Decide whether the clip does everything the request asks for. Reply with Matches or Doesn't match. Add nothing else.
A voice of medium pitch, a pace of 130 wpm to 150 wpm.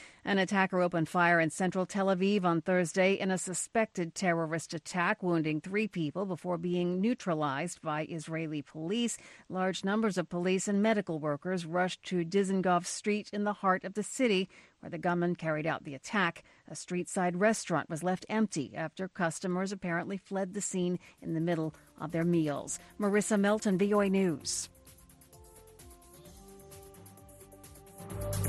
Matches